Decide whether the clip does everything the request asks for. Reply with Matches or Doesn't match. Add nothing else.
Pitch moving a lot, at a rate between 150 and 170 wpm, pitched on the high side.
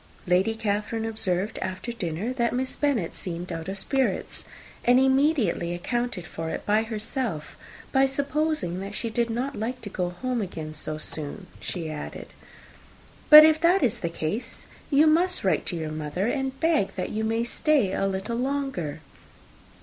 Matches